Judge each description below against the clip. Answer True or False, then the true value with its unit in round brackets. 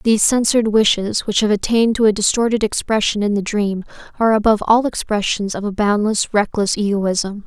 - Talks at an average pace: True (175 wpm)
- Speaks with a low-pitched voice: False (210 Hz)